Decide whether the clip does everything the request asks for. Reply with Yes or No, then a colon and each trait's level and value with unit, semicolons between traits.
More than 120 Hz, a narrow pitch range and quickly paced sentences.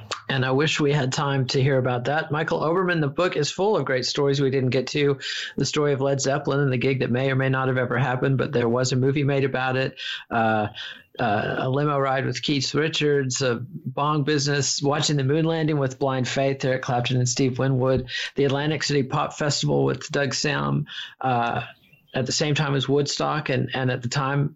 Yes: low, 135 Hz; narrow, 2.0 semitones; fast, 220 wpm